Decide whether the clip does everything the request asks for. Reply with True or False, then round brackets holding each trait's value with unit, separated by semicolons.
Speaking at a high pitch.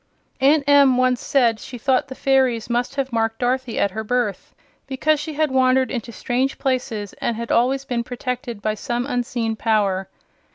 True (250 Hz)